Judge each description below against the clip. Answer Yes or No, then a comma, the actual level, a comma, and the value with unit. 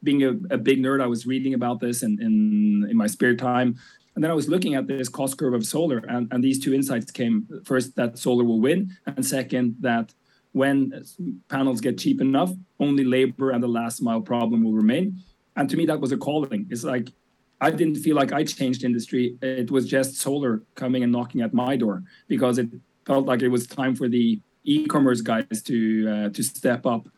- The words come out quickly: Yes, fast, 215 wpm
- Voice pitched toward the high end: No, low, 130 Hz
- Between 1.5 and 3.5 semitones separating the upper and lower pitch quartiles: Yes, average, 2.7 semitones